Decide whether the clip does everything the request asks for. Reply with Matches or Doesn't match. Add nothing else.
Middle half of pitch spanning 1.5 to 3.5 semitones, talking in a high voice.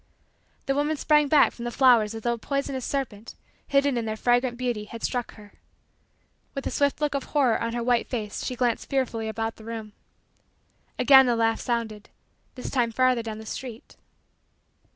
Matches